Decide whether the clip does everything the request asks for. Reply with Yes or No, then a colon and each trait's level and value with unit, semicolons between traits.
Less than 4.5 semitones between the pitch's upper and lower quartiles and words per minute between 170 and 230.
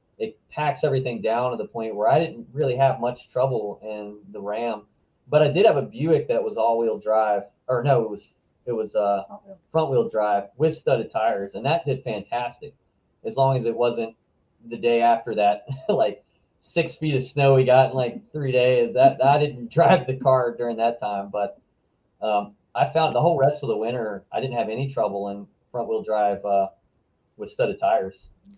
No: average, 5.2 semitones; fast, 205 wpm